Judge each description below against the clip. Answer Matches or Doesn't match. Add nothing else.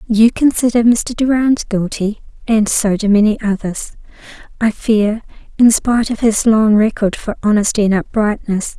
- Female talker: Matches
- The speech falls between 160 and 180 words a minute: Doesn't match